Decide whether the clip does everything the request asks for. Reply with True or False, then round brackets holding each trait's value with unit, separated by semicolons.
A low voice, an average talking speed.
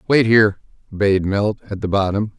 True (105 Hz; 175 wpm)